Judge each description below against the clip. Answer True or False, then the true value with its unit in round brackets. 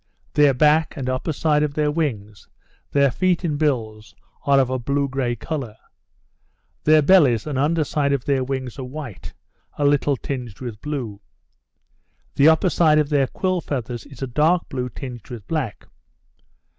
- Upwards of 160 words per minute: True (170 wpm)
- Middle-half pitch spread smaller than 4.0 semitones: True (3.4 semitones)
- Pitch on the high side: False (140 Hz)